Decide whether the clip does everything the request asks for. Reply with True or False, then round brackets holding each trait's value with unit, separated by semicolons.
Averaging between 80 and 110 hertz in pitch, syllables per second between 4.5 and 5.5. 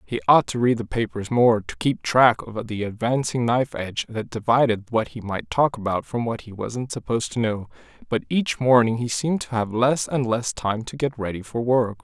False (120 Hz; 5.2 syllables/s)